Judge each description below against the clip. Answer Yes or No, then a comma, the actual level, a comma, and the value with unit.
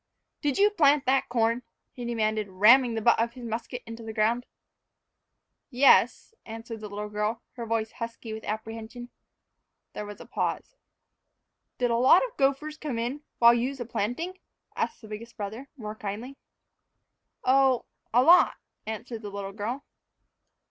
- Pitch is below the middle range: No, high, 235 Hz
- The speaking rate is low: No, average, 155 wpm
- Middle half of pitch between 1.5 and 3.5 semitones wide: Yes, average, 3.0 semitones